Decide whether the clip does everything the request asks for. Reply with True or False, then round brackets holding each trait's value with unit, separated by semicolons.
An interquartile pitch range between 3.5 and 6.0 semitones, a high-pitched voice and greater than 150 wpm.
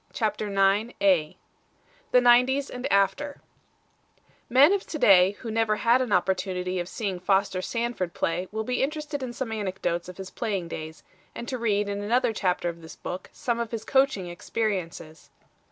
True (4.9 semitones; 210 Hz; 170 wpm)